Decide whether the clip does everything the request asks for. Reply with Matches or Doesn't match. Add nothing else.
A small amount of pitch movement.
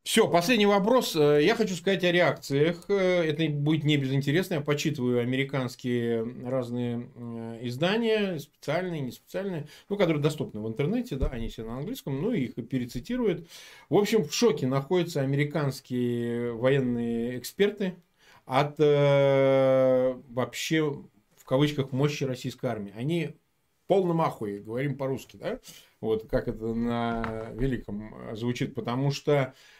Doesn't match